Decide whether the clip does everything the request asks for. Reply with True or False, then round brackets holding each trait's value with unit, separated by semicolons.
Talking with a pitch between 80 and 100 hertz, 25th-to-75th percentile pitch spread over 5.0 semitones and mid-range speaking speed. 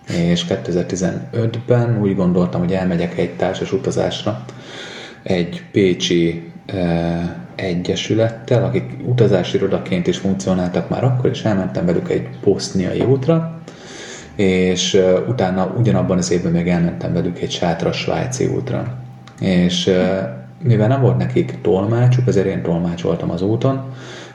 True (95 Hz; 5.5 semitones; 130 wpm)